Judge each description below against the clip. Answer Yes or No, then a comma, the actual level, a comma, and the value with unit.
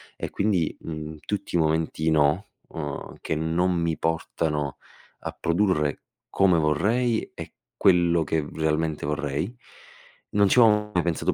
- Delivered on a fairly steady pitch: No, average, 3.5 semitones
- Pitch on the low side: Yes, very low, 80 Hz